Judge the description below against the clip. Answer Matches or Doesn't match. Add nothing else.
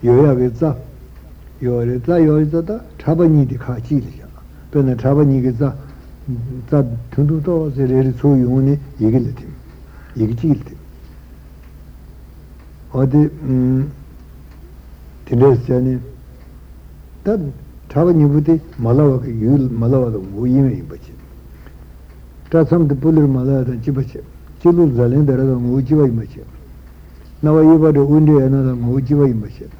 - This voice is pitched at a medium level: Doesn't match